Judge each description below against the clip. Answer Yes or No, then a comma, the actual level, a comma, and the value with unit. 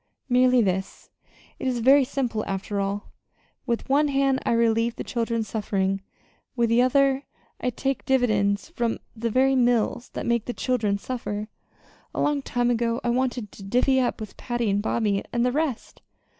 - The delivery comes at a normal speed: Yes, average, 170 wpm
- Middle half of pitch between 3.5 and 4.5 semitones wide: No, average, 3.1 semitones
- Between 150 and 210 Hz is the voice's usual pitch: No, high, 235 Hz